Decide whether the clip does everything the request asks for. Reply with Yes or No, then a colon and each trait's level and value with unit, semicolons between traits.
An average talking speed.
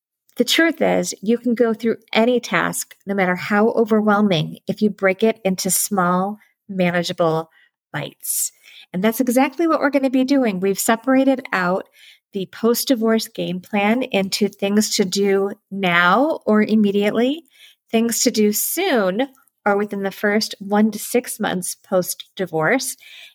Yes: average, 150 wpm